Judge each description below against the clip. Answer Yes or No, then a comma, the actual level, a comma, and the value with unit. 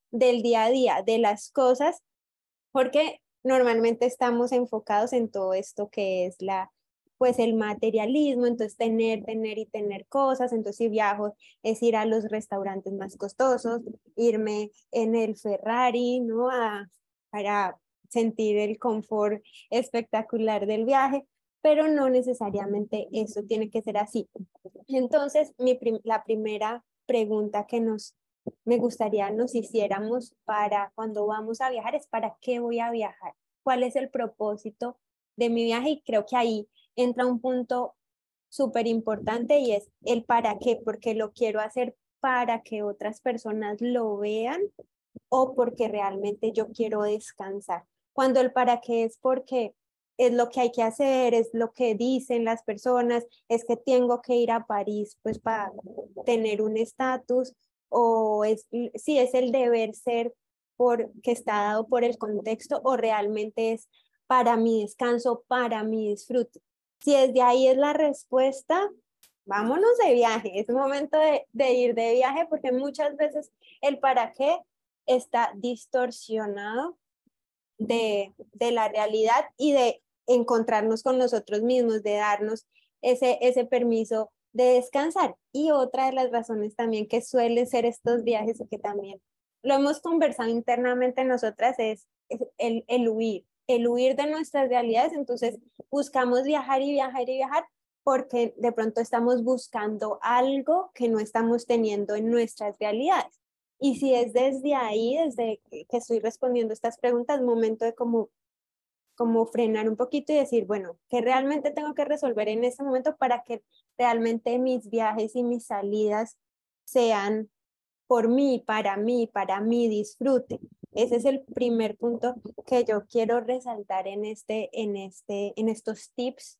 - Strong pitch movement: No, narrow, 2.6 semitones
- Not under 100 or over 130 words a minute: No, average, 150 wpm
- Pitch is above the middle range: Yes, high, 235 Hz